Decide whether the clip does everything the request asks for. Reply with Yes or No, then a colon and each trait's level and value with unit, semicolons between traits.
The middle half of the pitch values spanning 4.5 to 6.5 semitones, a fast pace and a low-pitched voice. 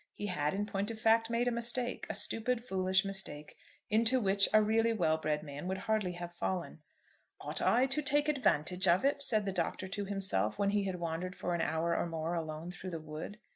No: average, 4.8 semitones; fast, 215 wpm; high, 195 Hz